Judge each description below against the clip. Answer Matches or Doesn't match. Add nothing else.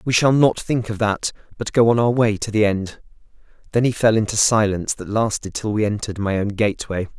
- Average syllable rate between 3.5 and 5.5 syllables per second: Doesn't match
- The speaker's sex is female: Doesn't match